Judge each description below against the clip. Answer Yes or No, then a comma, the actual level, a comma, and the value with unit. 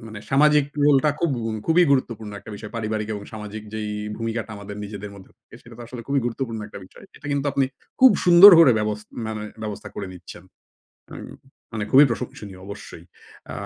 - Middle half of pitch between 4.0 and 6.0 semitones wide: Yes, average, 4.6 semitones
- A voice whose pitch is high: No, low, 110 Hz